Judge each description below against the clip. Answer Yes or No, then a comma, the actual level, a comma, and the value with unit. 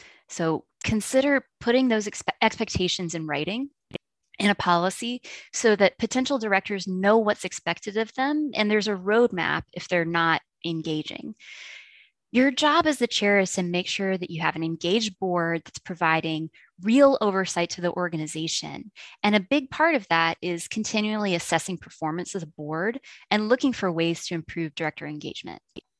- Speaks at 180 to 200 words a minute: No, average, 165 wpm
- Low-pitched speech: No, high, 195 Hz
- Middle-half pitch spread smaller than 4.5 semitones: No, average, 5.1 semitones